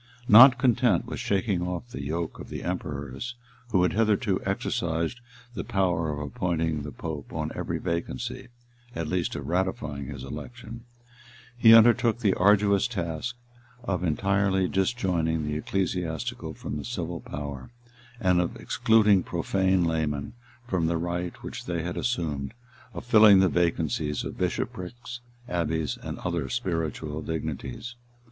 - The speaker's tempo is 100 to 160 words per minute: Yes, average, 140 wpm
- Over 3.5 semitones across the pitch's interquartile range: Yes, average, 4.2 semitones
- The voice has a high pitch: No, very low, 90 Hz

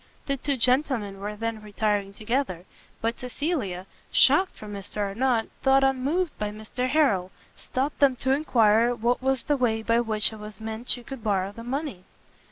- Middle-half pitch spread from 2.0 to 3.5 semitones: No, average, 4.1 semitones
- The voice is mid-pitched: No, high, 230 Hz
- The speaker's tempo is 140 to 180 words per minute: Yes, average, 175 wpm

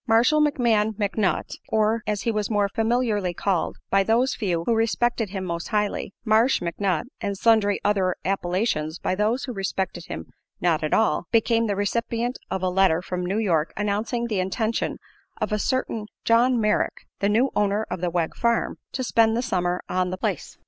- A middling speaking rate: Yes, average, 185 wpm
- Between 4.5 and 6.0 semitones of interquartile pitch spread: No, average, 3.7 semitones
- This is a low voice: No, high, 210 Hz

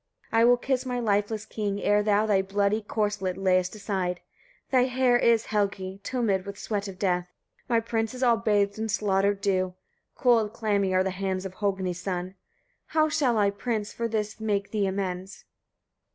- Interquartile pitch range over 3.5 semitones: No, average, 2.7 semitones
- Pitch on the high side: Yes, high, 205 Hz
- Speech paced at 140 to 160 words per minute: No, average, 180 wpm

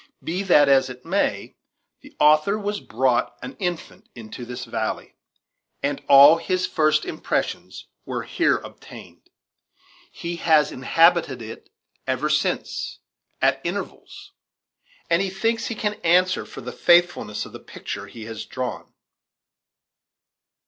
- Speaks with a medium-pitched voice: Yes, medium, 160 Hz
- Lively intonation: Yes, wide, 5.9 semitones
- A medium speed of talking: No, slow, 130 wpm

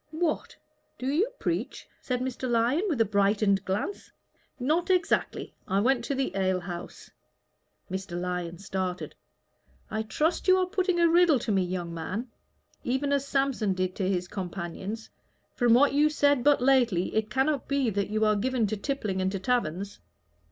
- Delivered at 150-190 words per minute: Yes, average, 165 wpm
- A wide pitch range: Yes, wide, 6.6 semitones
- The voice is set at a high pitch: Yes, high, 225 Hz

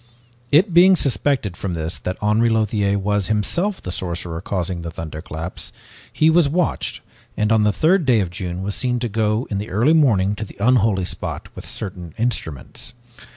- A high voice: No, low, 105 Hz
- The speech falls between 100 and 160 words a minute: No, average, 180 wpm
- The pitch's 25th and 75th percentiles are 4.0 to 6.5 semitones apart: Yes, average, 5.3 semitones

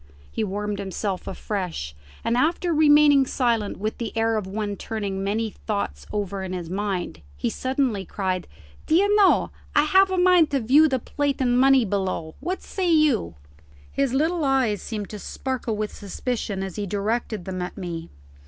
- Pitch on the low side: No, high, 220 Hz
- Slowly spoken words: No, average, 170 wpm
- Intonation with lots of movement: Yes, wide, 6.1 semitones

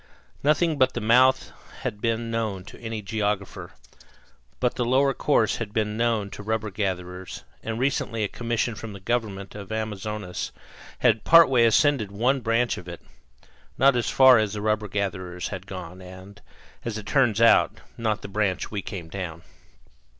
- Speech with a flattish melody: No, average, 3.2 semitones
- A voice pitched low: Yes, low, 110 Hz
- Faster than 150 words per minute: Yes, average, 170 wpm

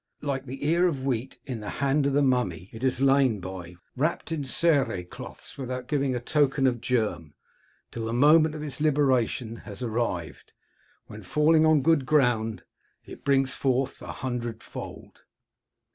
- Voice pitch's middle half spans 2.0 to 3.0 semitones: No, average, 3.9 semitones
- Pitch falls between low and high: No, low, 130 Hz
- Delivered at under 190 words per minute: Yes, average, 160 wpm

